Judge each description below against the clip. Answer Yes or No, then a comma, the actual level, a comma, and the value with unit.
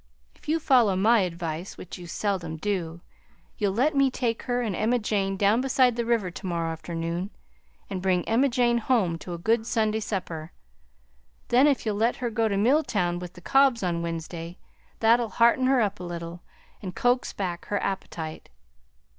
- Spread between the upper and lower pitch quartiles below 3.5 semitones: No, average, 5.3 semitones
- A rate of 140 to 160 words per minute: No, average, 180 wpm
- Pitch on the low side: No, high, 205 Hz